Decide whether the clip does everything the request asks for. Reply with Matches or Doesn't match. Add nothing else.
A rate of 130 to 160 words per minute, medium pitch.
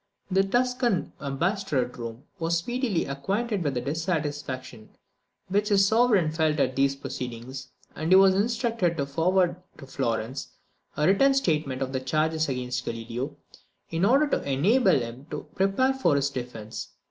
Matches